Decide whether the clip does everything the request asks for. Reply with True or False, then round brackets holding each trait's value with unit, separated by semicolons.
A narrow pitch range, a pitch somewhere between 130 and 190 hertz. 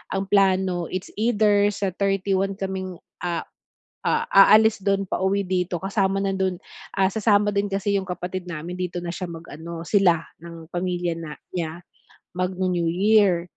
True (2.1 semitones; 185 Hz)